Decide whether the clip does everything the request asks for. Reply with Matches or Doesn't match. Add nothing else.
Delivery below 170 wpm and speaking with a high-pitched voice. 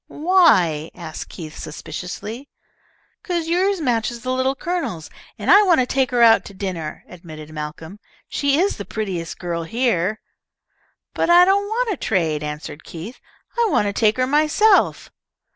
Matches